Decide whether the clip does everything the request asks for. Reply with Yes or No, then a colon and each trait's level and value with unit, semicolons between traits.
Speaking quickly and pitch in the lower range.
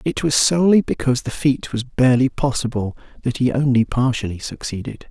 No: average, 165 wpm; low, 130 Hz